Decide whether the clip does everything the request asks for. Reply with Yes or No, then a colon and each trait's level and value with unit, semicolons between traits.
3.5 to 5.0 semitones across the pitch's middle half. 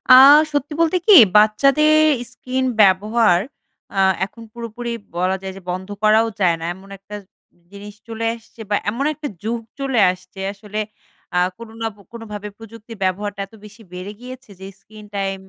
No: average, 3.0 semitones